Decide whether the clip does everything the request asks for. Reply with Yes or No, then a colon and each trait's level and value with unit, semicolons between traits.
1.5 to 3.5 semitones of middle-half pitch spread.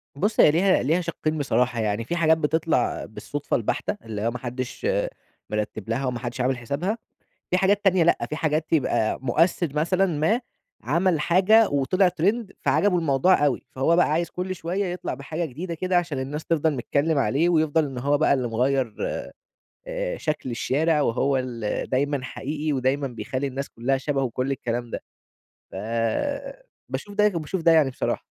No: average, 5.2 semitones